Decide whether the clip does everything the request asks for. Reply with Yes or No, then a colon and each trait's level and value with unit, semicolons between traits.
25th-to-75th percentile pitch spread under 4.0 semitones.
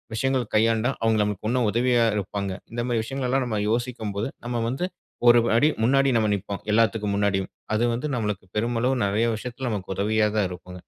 Yes: average, 3.0 semitones